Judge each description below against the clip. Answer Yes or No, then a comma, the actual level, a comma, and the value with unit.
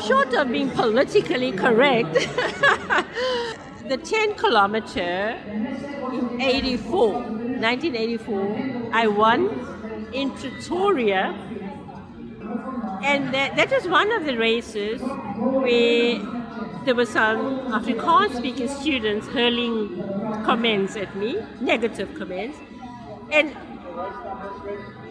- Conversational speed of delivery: No, slow, 85 wpm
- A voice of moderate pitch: No, high, 240 Hz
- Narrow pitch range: No, average, 3.8 semitones